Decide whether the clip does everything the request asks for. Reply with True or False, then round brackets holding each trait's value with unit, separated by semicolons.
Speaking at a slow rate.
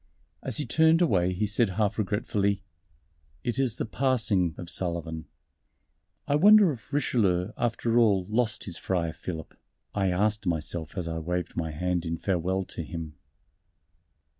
False (150 wpm)